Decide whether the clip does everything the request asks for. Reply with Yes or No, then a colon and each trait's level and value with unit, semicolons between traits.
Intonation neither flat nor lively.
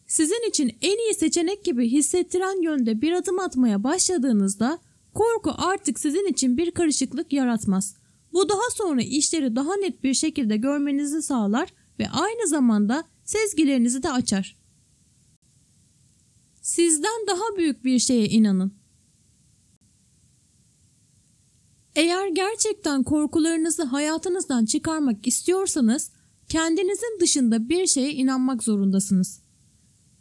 No: wide, 6.1 semitones